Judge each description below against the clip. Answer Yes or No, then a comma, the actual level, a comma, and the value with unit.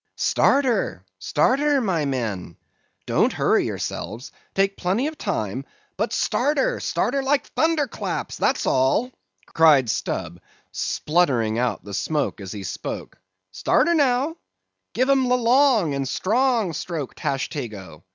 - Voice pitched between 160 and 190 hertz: Yes, medium, 185 Hz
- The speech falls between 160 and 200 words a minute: No, average, 140 wpm